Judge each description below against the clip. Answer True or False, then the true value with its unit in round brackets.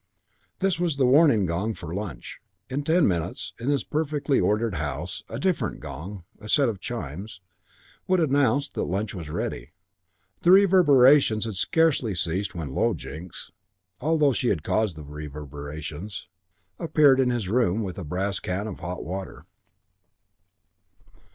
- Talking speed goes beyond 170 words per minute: False (150 wpm)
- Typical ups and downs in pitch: False (8.2 semitones)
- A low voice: True (105 Hz)